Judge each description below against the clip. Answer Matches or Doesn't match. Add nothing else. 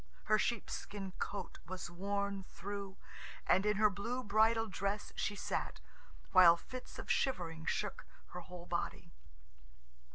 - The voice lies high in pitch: Matches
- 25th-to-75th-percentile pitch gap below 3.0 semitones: Matches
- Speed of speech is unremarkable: Doesn't match